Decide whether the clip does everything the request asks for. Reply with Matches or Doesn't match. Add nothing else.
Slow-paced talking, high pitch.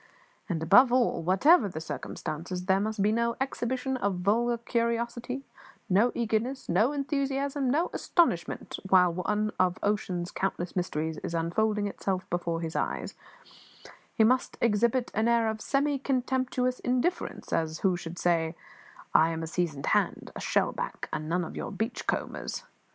Doesn't match